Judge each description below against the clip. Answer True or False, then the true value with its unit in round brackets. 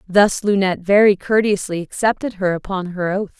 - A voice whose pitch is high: True (195 Hz)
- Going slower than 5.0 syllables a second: False (5.2 syllables/s)